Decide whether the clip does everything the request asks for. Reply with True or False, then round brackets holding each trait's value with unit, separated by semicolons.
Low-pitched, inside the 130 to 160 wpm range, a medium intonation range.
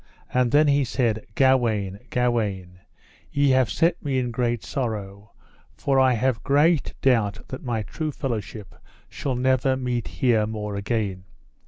True (120 Hz; 145 wpm; 3.8 semitones)